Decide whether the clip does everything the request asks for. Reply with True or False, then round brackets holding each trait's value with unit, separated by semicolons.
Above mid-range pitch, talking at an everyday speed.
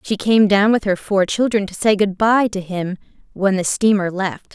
False (200 Hz; 225 wpm)